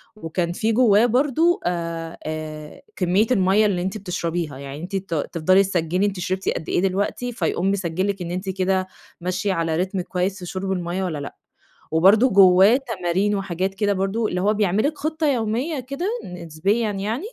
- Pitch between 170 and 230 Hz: Yes, high, 190 Hz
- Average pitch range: Yes, average, 3.2 semitones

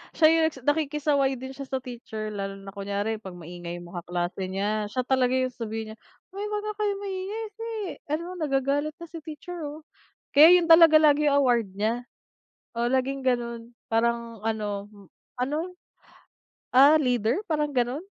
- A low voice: No, very high, 260 Hz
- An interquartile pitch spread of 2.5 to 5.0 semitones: No, wide, 5.6 semitones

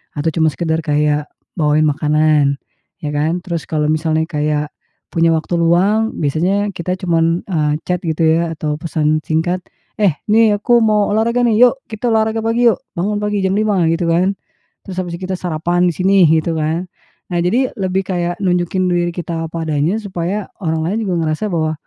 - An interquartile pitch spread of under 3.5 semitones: No, average, 3.8 semitones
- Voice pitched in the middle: Yes, medium, 175 Hz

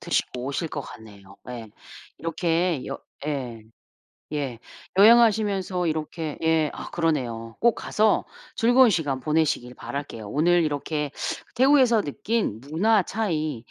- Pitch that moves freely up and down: Yes, wide, 6.8 semitones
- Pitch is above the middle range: No, medium, 155 Hz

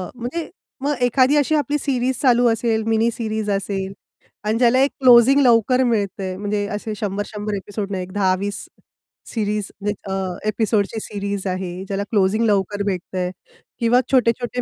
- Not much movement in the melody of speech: No, average, 3.5 semitones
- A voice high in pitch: Yes, high, 215 Hz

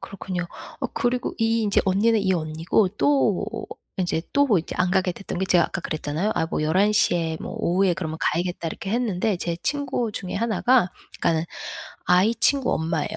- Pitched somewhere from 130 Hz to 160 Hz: No, high, 190 Hz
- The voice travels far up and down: No, average, 4.6 semitones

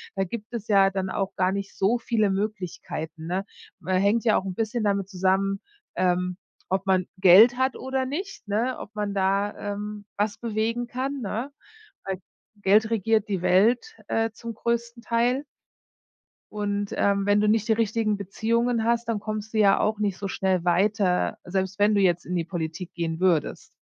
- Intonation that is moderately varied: Yes, average, 3.0 semitones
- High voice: Yes, high, 205 Hz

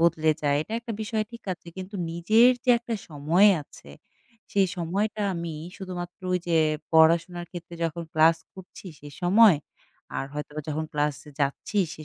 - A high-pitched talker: No, medium, 170 Hz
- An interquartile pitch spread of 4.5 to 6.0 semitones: No, average, 4.0 semitones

